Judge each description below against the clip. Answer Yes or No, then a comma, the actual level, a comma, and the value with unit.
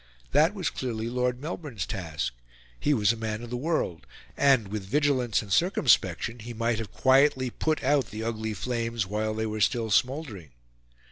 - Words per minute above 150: Yes, average, 175 wpm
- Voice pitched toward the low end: Yes, low, 115 Hz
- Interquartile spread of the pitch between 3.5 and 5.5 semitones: Yes, average, 3.8 semitones